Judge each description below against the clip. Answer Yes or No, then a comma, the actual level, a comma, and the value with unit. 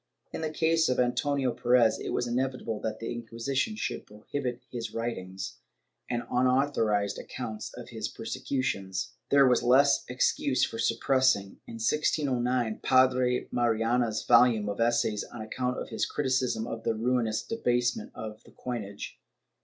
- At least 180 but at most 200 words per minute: No, average, 145 wpm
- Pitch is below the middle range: Yes, low, 120 Hz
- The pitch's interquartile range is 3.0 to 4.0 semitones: No, narrow, 2.5 semitones